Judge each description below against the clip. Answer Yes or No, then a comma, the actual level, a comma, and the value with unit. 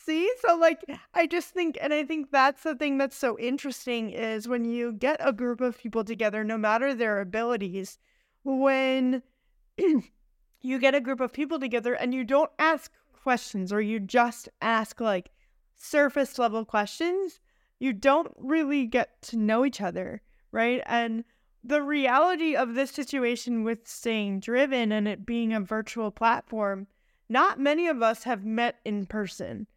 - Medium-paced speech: Yes, average, 165 wpm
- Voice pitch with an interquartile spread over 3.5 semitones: Yes, average, 3.9 semitones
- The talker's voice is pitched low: No, high, 245 Hz